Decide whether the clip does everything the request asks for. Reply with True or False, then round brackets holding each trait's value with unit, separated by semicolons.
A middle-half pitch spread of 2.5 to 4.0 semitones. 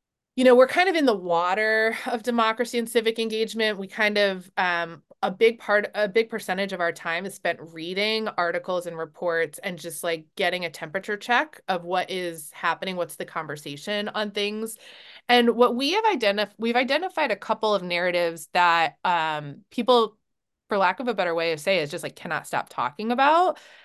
False (4.7 semitones)